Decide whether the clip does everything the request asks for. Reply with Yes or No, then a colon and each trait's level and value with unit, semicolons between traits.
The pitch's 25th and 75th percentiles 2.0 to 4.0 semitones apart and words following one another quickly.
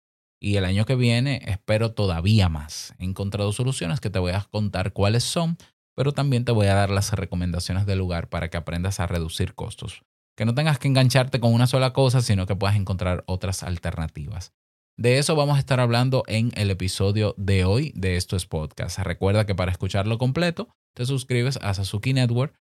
No: average, 5.2 semitones; fast, 195 wpm